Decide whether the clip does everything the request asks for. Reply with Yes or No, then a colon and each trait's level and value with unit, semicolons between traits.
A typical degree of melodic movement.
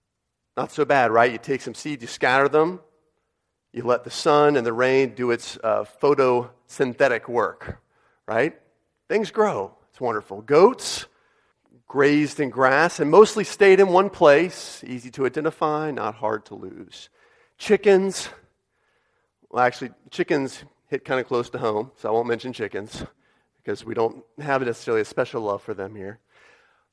Yes: average, 4.5 semitones